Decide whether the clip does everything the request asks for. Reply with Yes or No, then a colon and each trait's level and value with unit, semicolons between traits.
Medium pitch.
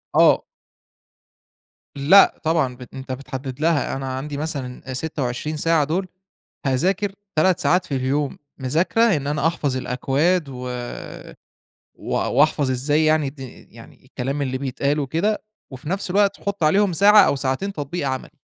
Yes: medium, 145 Hz